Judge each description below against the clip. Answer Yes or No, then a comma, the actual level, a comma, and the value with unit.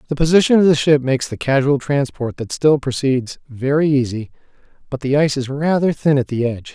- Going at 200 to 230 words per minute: Yes, fast, 205 wpm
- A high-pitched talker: No, medium, 140 Hz